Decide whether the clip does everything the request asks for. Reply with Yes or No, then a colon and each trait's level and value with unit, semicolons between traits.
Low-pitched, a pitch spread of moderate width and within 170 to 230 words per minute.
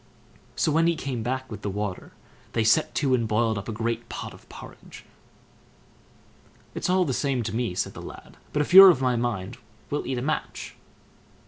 Yes: low, 120 Hz; average, 4.5 semitones; average, 200 wpm